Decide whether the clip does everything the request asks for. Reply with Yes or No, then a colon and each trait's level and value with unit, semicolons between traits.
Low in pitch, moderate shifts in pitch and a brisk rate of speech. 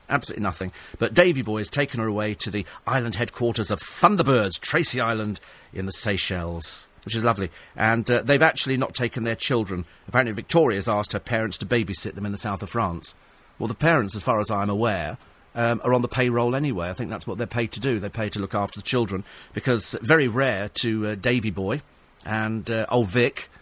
Yes: low, 115 Hz; average, 3.0 semitones; fast, 220 wpm